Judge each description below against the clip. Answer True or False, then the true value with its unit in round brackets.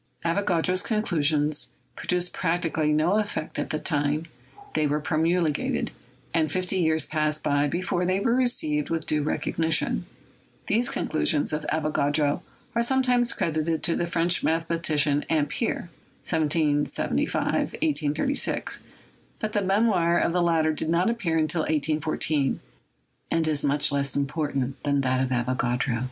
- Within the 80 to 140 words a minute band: True (135 wpm)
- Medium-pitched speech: True (160 Hz)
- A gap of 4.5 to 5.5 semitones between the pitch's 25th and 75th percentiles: False (3.1 semitones)